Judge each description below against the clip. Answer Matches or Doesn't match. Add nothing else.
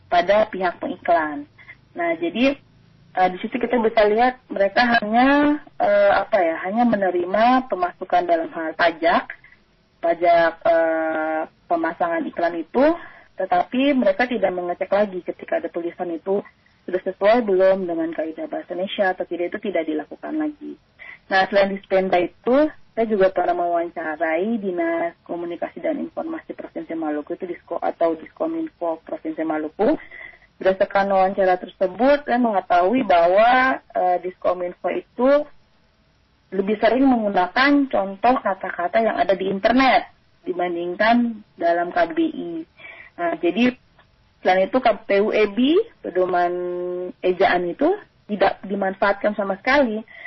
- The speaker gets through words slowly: Doesn't match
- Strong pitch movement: Matches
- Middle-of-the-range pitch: Doesn't match